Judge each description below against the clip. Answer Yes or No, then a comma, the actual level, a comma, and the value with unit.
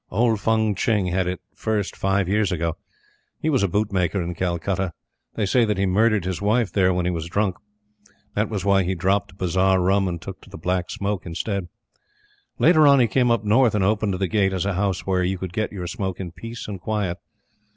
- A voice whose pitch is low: Yes, very low, 95 Hz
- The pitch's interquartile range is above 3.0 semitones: No, average, 2.7 semitones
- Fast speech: Yes, fast, 220 wpm